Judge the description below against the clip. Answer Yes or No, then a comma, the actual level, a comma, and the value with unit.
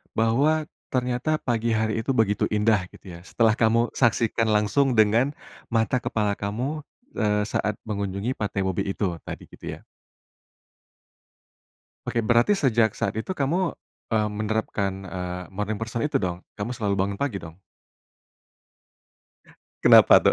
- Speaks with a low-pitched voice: Yes, low, 110 Hz